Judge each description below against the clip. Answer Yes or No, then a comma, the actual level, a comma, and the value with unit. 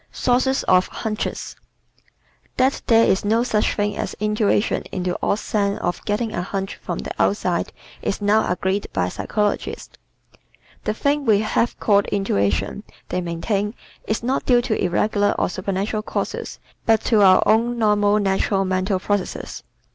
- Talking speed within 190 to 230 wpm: No, average, 155 wpm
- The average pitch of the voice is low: No, high, 205 Hz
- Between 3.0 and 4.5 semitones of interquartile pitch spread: No, narrow, 2.4 semitones